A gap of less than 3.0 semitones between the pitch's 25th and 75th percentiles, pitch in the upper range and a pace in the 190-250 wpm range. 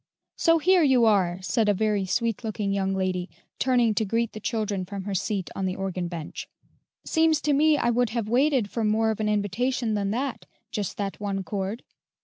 No: average, 3.8 semitones; high, 215 Hz; average, 200 wpm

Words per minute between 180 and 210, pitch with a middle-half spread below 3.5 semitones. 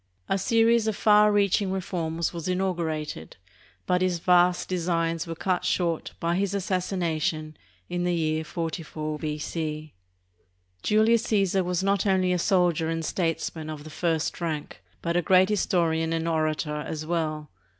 No: average, 150 wpm; average, 2.8 semitones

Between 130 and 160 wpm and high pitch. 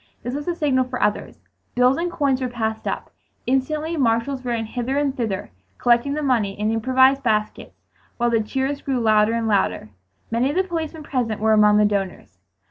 No: average, 190 wpm; high, 245 Hz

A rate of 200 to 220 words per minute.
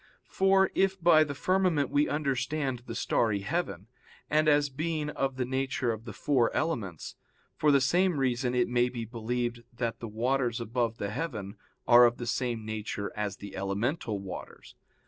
No: average, 170 wpm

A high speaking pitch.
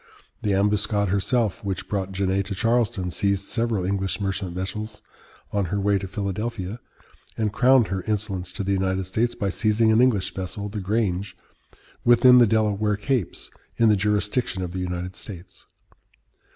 No: low, 100 Hz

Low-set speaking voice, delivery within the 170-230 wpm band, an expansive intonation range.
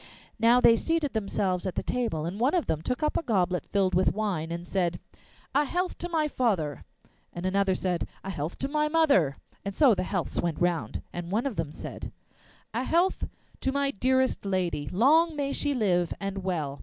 No: high, 200 Hz; average, 200 wpm; wide, 7.7 semitones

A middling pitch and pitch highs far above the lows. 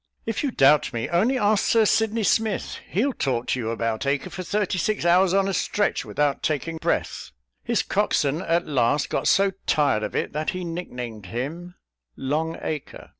Yes: medium, 165 Hz; wide, 6.5 semitones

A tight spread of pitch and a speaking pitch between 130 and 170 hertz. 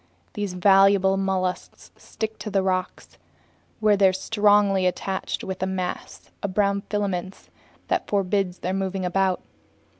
No: narrow, 1.4 semitones; high, 195 Hz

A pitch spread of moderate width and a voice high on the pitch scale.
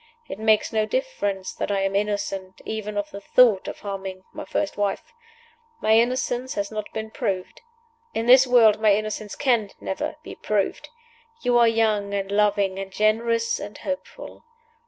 No: narrow, 2.3 semitones; high, 210 Hz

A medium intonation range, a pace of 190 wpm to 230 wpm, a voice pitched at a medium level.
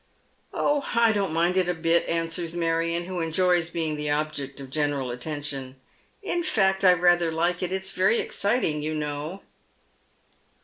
No: average, 3.4 semitones; average, 170 wpm; medium, 165 Hz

